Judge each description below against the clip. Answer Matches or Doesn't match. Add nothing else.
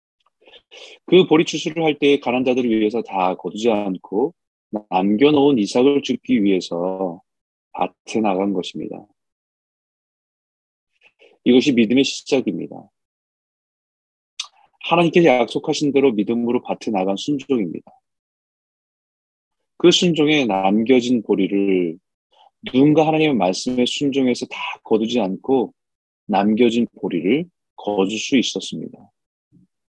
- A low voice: Matches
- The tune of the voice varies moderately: Doesn't match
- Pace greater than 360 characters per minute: Doesn't match